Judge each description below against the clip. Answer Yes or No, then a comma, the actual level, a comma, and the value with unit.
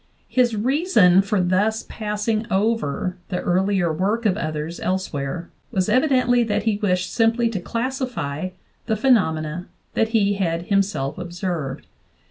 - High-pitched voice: Yes, high, 200 Hz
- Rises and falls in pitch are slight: No, average, 4.3 semitones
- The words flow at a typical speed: No, slow, 130 wpm